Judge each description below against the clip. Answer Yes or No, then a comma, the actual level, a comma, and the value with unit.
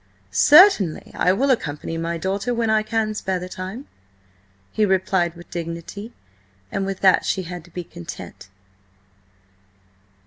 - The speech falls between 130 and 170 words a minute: Yes, average, 140 wpm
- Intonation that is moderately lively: Yes, average, 3.9 semitones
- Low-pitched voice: No, high, 190 Hz